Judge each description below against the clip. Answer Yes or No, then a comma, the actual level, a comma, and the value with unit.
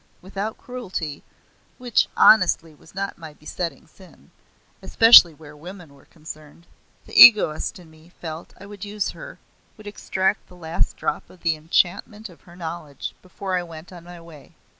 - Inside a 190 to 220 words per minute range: No, average, 160 wpm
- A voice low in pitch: No, medium, 175 Hz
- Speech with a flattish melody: No, average, 3.8 semitones